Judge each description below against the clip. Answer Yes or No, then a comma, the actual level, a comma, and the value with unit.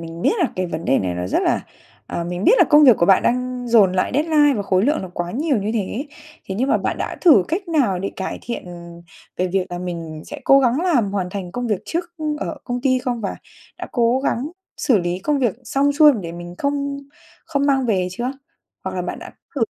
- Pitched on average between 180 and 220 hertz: No, high, 235 Hz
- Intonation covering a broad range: Yes, wide, 7.4 semitones